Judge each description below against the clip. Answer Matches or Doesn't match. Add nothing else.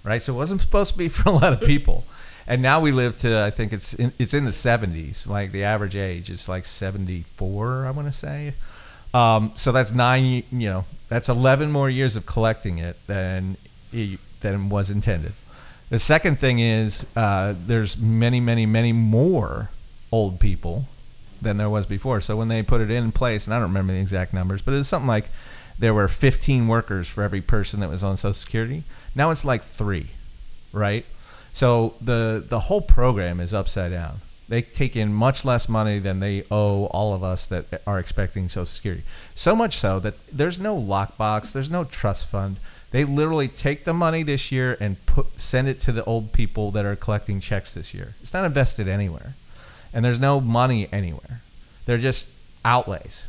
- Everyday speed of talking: Matches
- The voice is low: Matches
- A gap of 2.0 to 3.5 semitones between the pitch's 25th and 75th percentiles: Doesn't match